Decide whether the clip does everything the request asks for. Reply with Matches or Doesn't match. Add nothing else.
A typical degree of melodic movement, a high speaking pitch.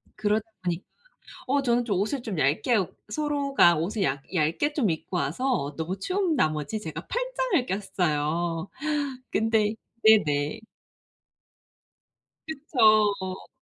Doesn't match